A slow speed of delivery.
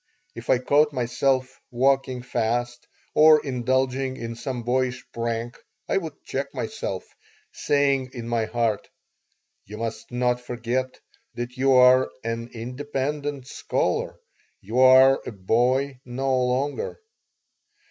Yes: slow, 120 wpm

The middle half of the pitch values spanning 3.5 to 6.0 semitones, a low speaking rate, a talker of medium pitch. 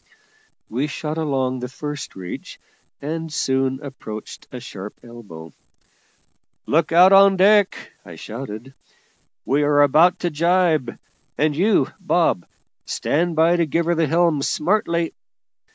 Yes: average, 4.4 semitones; slow, 130 wpm; medium, 150 Hz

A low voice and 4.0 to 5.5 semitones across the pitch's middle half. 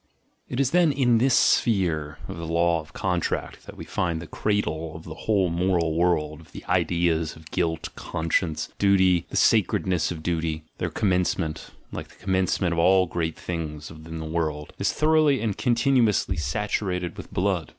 No: very low, 85 Hz; average, 3.4 semitones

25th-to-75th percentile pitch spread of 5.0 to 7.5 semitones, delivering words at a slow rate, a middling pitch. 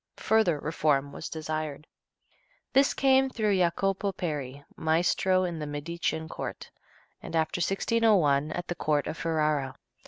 No: average, 4.1 semitones; slow, 130 wpm; medium, 160 Hz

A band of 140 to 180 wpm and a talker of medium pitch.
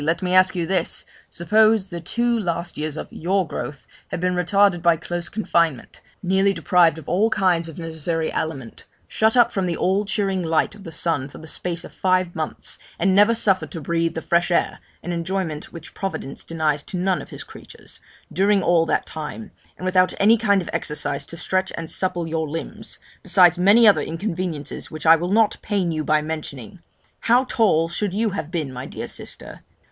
No: average, 195 wpm; medium, 175 Hz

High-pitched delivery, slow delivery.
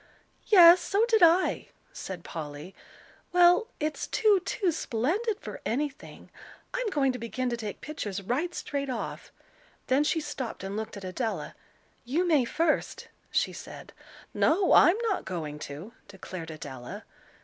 No: very high, 275 Hz; average, 145 wpm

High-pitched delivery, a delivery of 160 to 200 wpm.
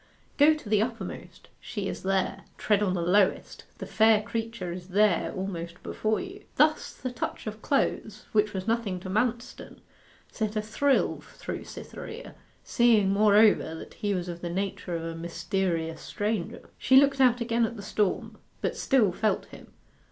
Yes: high, 210 Hz; average, 170 wpm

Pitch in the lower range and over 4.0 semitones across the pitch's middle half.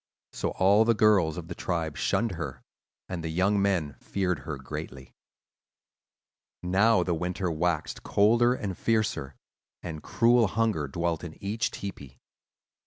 Yes: very low, 90 Hz; average, 4.6 semitones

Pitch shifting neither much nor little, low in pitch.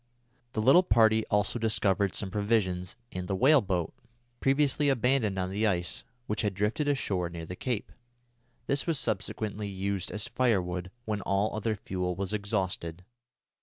Yes: average, 3.6 semitones; low, 105 Hz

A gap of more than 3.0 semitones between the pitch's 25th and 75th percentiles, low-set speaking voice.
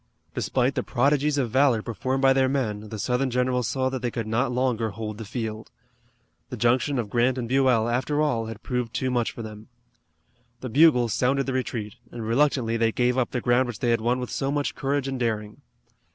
No: narrow, 2.6 semitones; low, 125 Hz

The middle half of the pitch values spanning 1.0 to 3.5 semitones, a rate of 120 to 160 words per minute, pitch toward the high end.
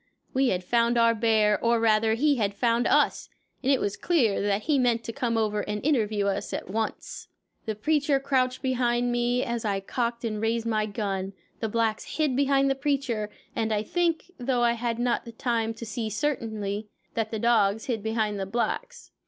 No: average, 2.8 semitones; average, 195 wpm; high, 230 Hz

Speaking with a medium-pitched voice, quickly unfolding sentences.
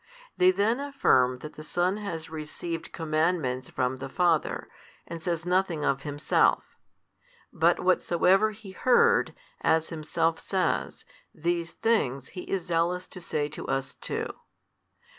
No: medium, 170 Hz; slow, 135 wpm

